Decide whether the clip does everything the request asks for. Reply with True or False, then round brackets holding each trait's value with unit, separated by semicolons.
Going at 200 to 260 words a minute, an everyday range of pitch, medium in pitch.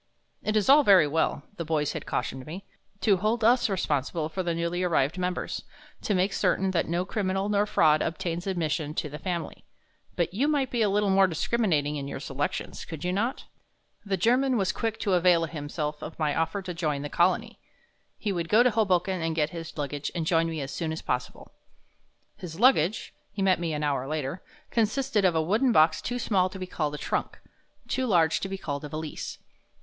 True (205 wpm; 4.4 semitones; 175 Hz)